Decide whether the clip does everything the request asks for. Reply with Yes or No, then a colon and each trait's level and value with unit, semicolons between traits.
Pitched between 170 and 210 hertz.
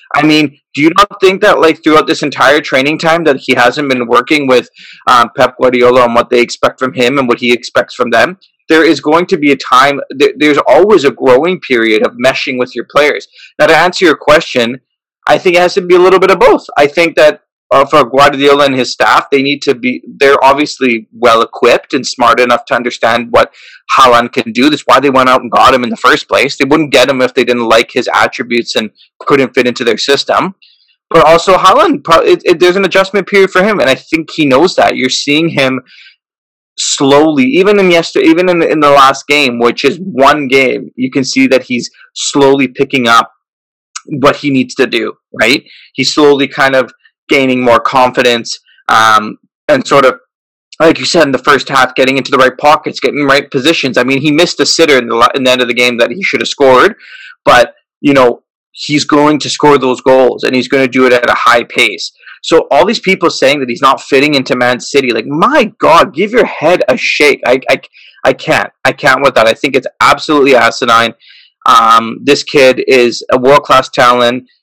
No: medium, 140 Hz